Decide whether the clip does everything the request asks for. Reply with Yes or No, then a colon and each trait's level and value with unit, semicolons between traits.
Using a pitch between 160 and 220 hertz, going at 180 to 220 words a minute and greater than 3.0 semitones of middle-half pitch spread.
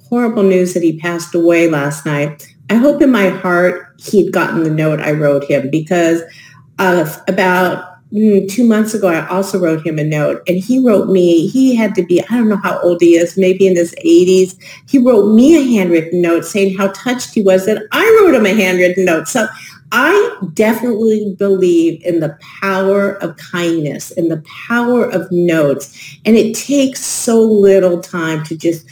Yes: medium, 185 Hz; average, 190 wpm; average, 4.0 semitones